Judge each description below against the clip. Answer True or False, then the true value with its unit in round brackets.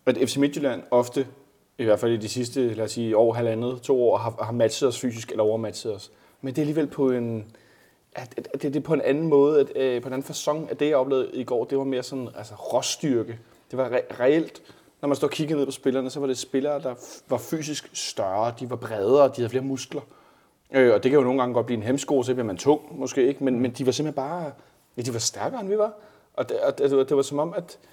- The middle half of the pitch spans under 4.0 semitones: True (2.7 semitones)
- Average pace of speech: False (265 wpm)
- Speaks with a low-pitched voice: True (130 Hz)